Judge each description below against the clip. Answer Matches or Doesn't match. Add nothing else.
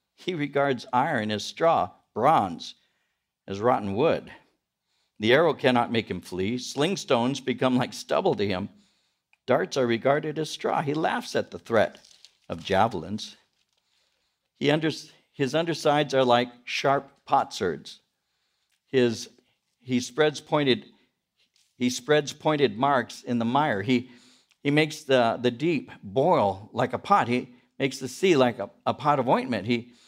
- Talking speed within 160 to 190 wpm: Doesn't match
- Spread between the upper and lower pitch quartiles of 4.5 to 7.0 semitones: Doesn't match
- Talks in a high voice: Doesn't match